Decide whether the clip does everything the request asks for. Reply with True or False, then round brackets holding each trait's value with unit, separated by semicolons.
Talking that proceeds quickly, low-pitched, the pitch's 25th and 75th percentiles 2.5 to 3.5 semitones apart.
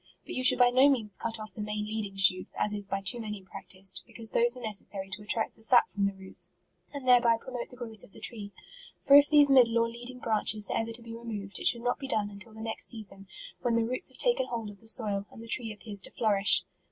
False (260 wpm; 225 Hz; 2.8 semitones)